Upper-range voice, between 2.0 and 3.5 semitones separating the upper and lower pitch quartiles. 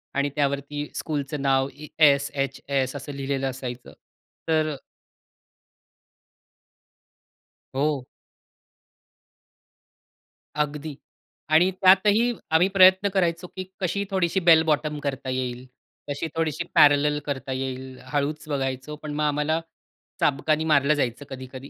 No: medium, 145 Hz; average, 2.8 semitones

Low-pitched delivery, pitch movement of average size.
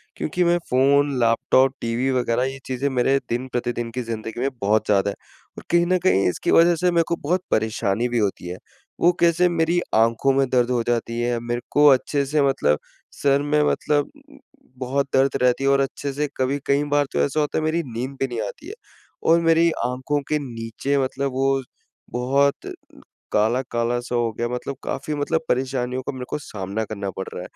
Yes: low, 130 Hz; average, 3.4 semitones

